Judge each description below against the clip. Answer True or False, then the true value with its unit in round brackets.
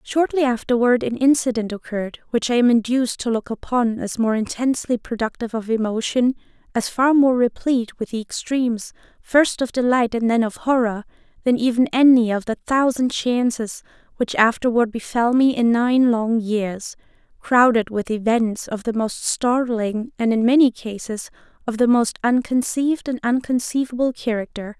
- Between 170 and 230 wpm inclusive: False (155 wpm)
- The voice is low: False (235 Hz)